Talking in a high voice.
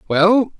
Yes: high, 205 Hz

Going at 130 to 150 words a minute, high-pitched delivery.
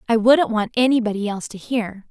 No: average, 200 wpm; high, 225 Hz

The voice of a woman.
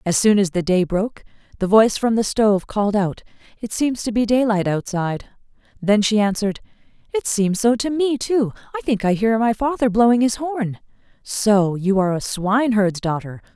Yes: female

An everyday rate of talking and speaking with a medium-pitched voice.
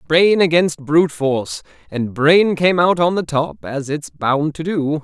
Yes: average, 165 wpm; medium, 150 Hz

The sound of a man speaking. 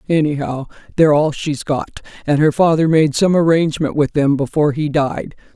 No: female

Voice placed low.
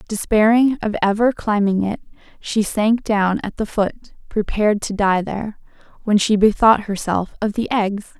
No: high, 210 Hz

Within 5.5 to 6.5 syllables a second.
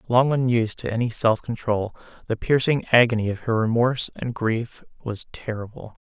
No: 5.2 syllables/s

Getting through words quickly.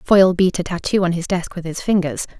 Yes: fast, 250 wpm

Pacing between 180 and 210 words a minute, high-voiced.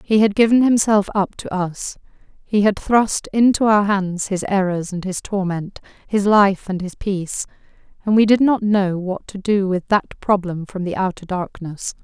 Yes: average, 190 wpm; high, 195 Hz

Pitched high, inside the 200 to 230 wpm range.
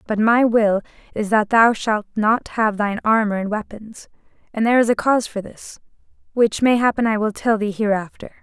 No: high, 220 Hz; average, 190 wpm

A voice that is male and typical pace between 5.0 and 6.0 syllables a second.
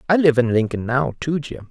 Yes: male; 5.5 syllables/s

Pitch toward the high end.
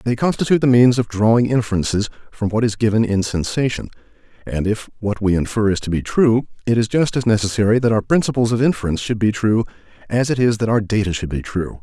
No: low, 110 Hz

